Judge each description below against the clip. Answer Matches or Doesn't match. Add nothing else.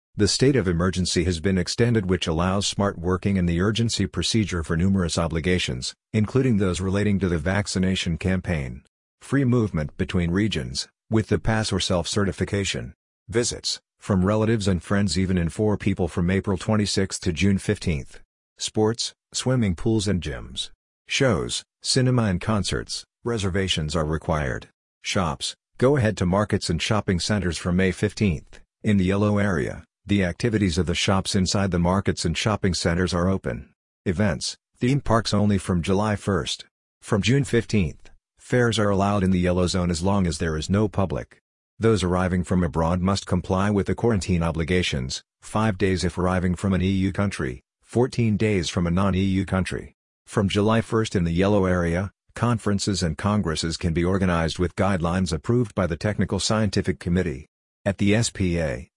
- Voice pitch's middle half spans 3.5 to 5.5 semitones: Doesn't match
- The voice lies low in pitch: Matches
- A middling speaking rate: Matches